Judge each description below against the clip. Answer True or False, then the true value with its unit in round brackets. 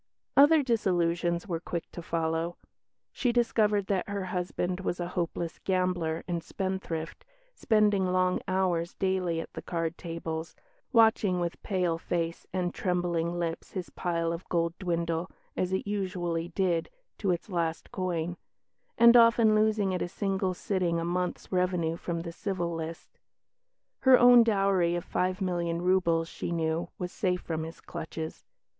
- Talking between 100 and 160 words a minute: True (150 wpm)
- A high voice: False (180 Hz)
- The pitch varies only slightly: True (2.2 semitones)